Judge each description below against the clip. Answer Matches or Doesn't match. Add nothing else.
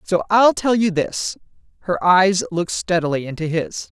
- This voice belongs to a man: Doesn't match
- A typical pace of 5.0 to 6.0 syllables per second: Doesn't match